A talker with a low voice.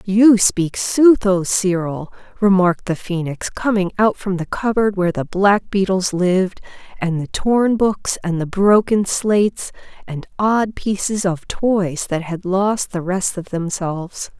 No: high, 190 Hz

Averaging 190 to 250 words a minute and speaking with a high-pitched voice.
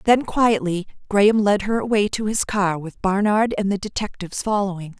No: average, 180 wpm; high, 200 Hz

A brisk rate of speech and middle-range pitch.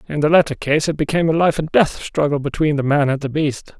Yes: fast, 270 wpm; medium, 150 Hz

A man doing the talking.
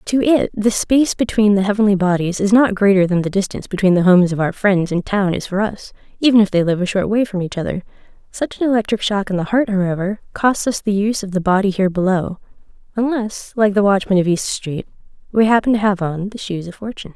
No: female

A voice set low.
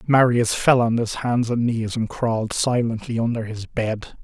Yes: low, 115 Hz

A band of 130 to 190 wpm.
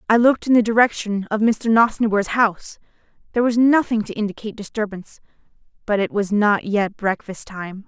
Yes: average, 160 wpm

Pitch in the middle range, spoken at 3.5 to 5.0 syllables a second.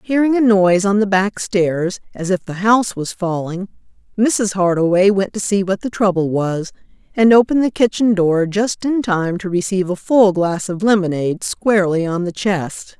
No: high, 195 Hz; 4.8 syllables/s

